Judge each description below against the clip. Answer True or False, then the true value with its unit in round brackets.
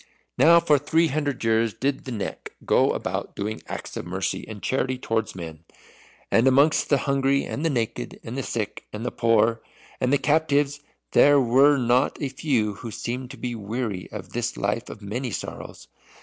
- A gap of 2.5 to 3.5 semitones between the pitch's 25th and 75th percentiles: False (4.1 semitones)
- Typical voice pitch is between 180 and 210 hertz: False (125 Hz)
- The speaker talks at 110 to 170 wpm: False (185 wpm)